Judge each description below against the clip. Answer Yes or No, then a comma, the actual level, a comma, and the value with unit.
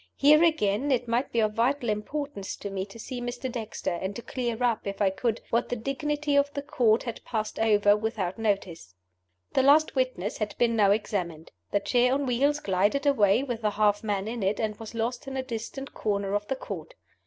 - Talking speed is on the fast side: Yes, fast, 210 wpm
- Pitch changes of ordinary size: Yes, average, 4.2 semitones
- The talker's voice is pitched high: Yes, high, 225 Hz